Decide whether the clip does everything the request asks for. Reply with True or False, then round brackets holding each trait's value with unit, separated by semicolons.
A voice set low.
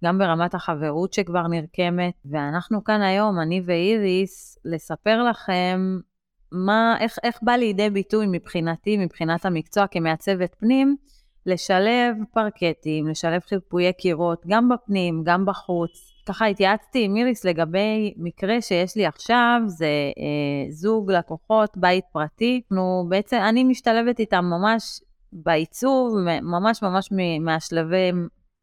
False (185 Hz)